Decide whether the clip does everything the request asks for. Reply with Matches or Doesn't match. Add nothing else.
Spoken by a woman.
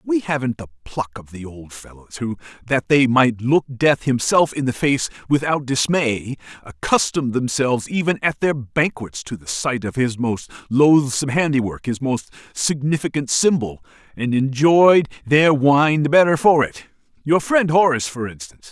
Doesn't match